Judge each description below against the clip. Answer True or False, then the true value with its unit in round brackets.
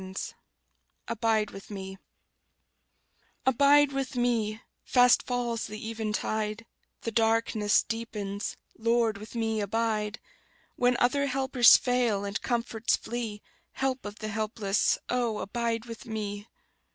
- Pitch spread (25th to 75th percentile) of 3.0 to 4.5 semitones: False (2.4 semitones)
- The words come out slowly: True (120 wpm)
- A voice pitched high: True (225 Hz)